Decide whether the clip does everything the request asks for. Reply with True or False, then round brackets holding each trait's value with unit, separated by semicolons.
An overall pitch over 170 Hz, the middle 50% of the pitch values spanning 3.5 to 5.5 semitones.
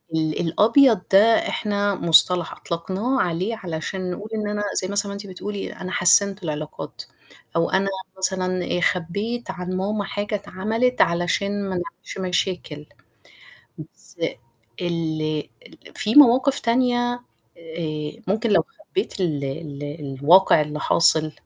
True (185 Hz; 3.9 semitones)